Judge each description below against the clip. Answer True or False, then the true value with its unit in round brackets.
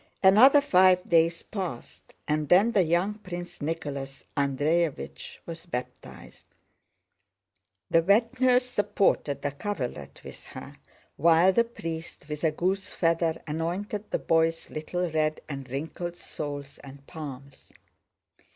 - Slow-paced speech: True (125 wpm)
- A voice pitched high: False (165 Hz)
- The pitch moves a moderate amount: True (4.5 semitones)